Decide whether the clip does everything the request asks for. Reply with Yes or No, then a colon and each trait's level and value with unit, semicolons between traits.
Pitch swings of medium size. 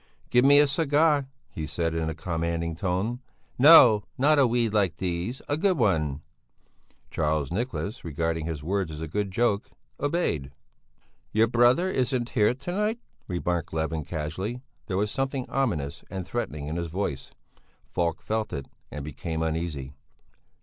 No: wide, 7.4 semitones